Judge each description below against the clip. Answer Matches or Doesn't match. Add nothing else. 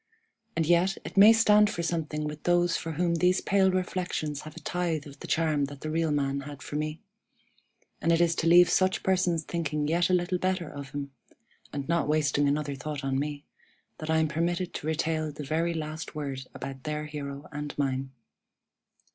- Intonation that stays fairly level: Doesn't match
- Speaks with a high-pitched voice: Doesn't match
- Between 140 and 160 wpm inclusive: Doesn't match